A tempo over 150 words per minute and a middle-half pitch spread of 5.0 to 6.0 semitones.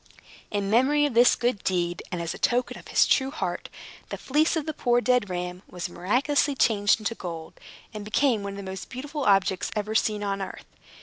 Yes: fast, 205 wpm; average, 5.3 semitones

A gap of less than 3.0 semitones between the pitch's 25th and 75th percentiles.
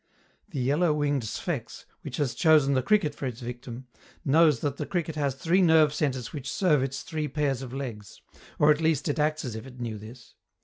No: average, 3.5 semitones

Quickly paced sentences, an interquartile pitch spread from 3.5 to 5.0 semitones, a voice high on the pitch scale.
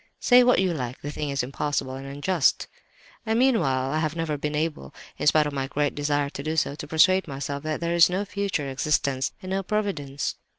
No: fast, 210 wpm; average, 4.5 semitones; medium, 150 Hz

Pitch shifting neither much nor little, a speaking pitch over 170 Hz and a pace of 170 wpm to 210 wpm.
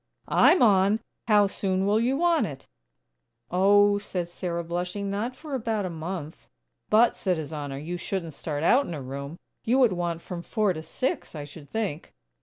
Yes: average, 4.6 semitones; medium, 185 Hz; average, 185 wpm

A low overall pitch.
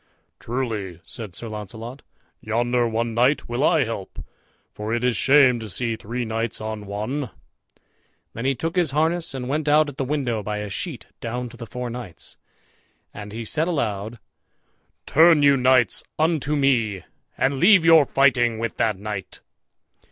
Yes: low, 120 Hz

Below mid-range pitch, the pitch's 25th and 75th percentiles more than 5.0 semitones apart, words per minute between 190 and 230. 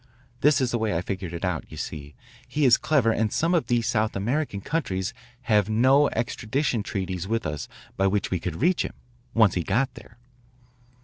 Yes: low, 110 Hz; wide, 5.5 semitones; average, 195 wpm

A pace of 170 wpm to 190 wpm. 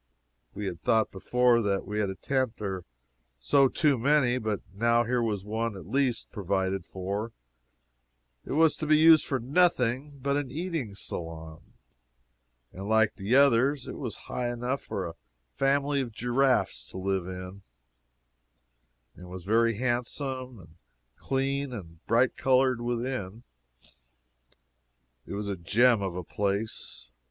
No: average, 145 wpm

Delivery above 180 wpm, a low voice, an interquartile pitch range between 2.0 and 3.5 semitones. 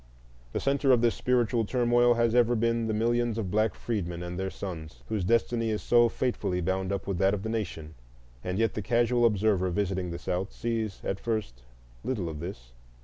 No: average, 200 wpm; low, 110 Hz; average, 4.0 semitones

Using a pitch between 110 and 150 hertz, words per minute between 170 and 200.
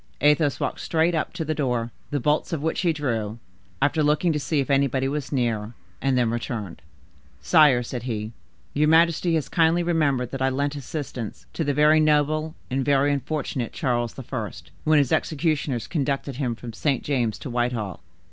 Yes: medium, 140 Hz; average, 180 wpm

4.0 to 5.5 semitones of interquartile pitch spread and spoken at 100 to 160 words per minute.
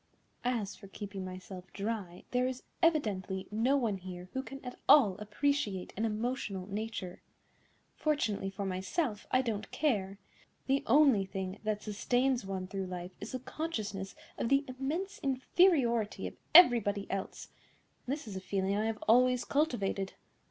Yes: average, 5.0 semitones; average, 150 wpm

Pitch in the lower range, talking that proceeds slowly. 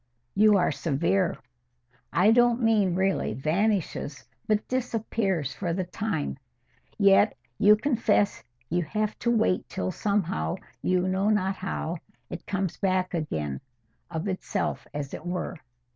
No: high, 190 Hz; slow, 130 wpm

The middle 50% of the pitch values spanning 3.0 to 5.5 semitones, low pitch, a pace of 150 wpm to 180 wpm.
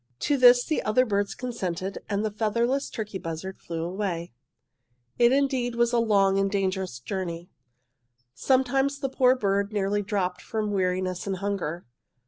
No: average, 4.4 semitones; high, 205 Hz; average, 155 wpm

